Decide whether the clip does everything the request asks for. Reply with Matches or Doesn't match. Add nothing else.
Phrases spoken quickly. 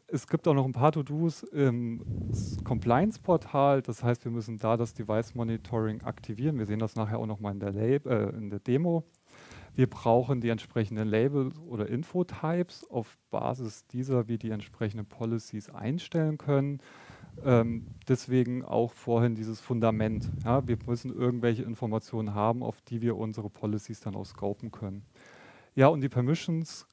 Doesn't match